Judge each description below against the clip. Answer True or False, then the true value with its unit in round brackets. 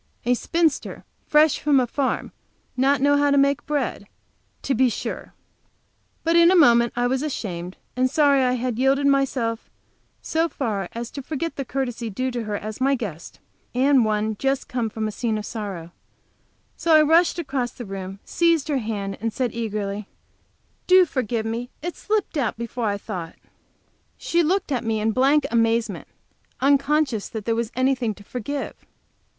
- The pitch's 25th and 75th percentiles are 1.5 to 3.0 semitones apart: False (4.3 semitones)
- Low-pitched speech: False (250 Hz)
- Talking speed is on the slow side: False (175 wpm)